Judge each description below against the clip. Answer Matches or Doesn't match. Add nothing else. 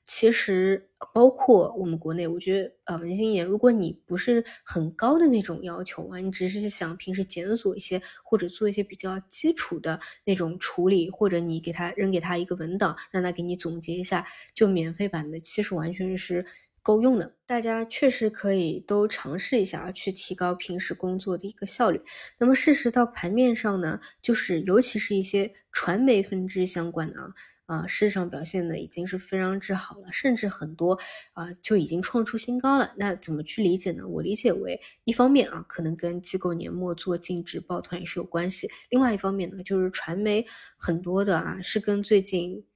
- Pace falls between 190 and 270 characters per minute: Doesn't match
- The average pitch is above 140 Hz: Matches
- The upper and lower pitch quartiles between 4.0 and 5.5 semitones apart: Doesn't match